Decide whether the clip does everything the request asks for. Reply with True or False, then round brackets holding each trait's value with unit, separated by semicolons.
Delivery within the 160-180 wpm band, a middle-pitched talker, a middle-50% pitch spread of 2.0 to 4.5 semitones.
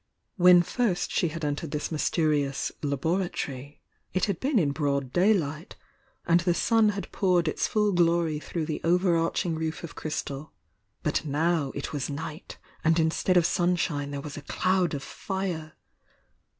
True (165 wpm; 165 Hz; 3.3 semitones)